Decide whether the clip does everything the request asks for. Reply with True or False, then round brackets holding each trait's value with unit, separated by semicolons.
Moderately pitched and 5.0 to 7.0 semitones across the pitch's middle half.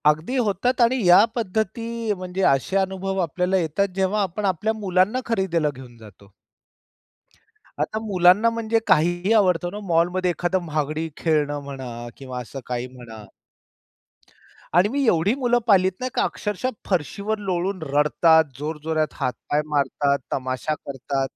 True (180 Hz; 5.5 semitones)